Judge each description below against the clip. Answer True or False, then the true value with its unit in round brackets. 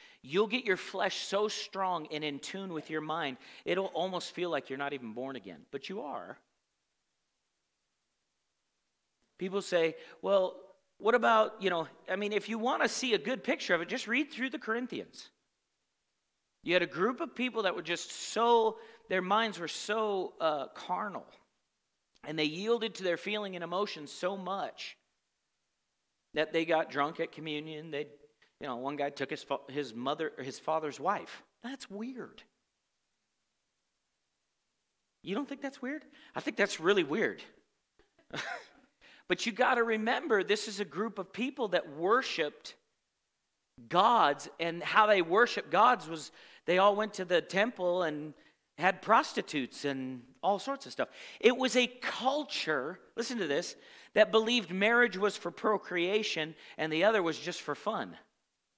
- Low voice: False (195 Hz)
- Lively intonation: True (6.3 semitones)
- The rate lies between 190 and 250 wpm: False (165 wpm)